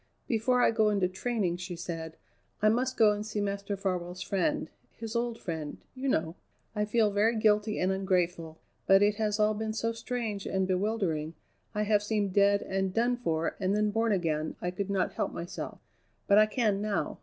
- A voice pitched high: Yes, high, 205 Hz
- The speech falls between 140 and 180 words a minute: No, average, 190 wpm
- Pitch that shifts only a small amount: No, average, 3.0 semitones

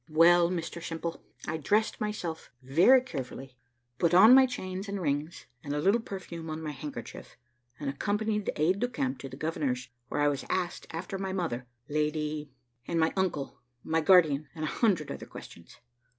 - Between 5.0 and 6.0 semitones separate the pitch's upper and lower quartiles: No, average, 4.5 semitones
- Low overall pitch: No, medium, 165 Hz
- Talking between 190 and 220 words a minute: No, average, 180 wpm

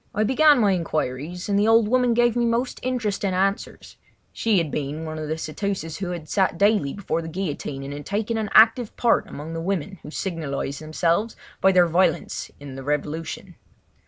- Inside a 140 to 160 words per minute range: No, average, 185 wpm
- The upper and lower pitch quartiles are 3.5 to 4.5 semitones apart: No, wide, 5.5 semitones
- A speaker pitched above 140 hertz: Yes, medium, 185 Hz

